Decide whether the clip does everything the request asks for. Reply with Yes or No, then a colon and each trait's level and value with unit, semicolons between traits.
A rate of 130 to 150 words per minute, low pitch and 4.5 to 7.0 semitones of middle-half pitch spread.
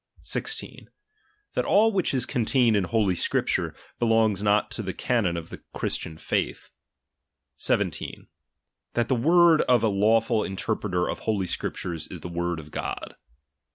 Yes: average, 145 wpm; low, 110 Hz; average, 4.9 semitones